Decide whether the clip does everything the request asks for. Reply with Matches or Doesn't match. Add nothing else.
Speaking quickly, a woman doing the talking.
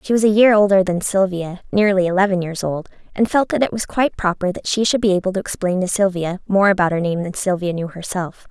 Matches